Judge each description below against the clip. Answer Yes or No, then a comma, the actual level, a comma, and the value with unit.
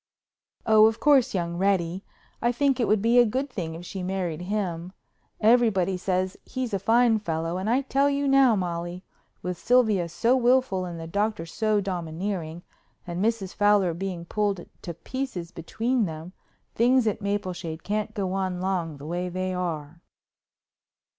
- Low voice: No, high, 195 Hz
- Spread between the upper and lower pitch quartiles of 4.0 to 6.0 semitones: Yes, average, 4.5 semitones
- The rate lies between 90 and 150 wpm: No, average, 165 wpm